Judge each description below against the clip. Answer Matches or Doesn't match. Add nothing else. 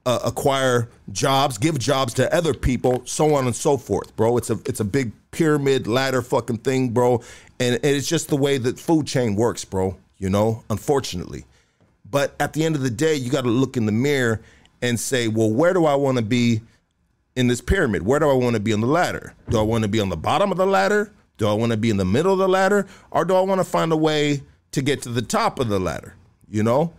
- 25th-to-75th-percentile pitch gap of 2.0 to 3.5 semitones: Doesn't match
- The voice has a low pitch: Matches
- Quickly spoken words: Matches